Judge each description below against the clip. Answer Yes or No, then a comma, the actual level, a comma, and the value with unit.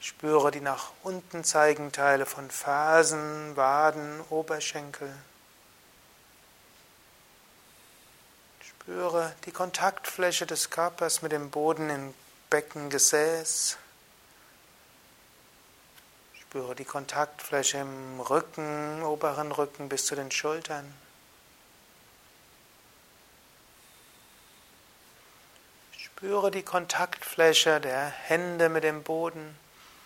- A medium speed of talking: No, slow, 80 wpm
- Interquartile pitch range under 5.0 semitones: Yes, narrow, 2.4 semitones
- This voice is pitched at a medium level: Yes, medium, 150 Hz